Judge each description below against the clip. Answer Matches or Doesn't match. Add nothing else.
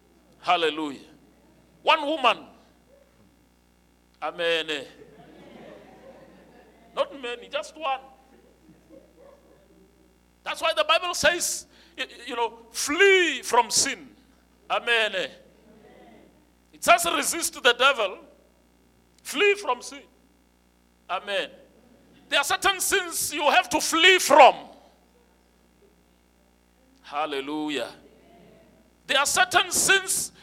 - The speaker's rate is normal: Doesn't match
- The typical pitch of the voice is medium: Doesn't match